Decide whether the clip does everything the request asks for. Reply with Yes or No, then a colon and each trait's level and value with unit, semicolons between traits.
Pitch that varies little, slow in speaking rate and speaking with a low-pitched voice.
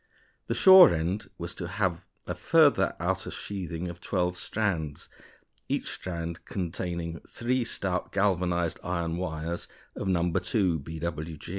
Yes: narrow, 2.0 semitones; slow, 130 wpm; very low, 85 Hz